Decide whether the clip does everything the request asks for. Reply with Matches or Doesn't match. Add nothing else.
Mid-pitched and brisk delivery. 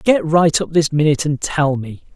Matches